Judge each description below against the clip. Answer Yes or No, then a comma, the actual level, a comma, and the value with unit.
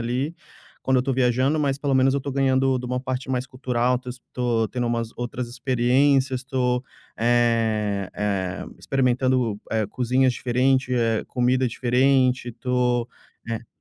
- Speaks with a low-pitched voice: Yes, low, 125 Hz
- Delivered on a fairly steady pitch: Yes, narrow, 1.6 semitones